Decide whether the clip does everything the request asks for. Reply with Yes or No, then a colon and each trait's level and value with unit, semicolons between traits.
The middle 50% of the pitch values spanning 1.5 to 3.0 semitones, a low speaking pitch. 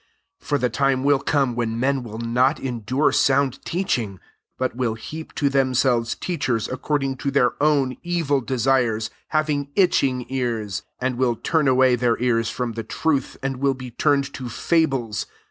Yes: average, 2.7 semitones; low, 130 Hz